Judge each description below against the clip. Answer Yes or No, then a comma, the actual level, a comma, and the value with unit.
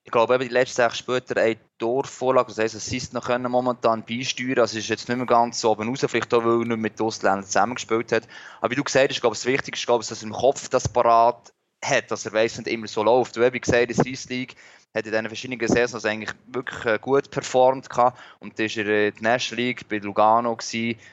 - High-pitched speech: No, low, 115 Hz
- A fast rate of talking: Yes, fast, 230 wpm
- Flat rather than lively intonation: Yes, narrow, 2.1 semitones